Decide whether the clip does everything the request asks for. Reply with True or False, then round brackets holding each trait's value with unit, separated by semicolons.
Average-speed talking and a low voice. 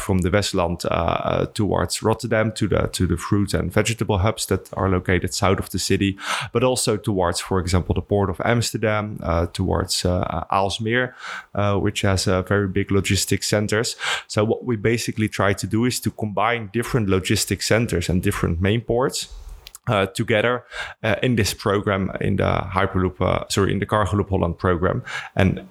True (180 wpm; 100 Hz)